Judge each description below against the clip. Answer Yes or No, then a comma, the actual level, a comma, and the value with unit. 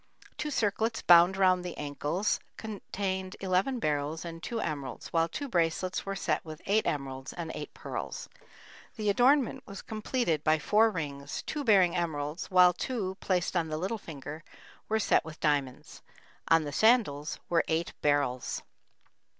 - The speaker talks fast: No, average, 155 wpm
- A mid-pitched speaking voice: Yes, medium, 175 Hz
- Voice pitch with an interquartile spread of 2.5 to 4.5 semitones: No, average, 5.1 semitones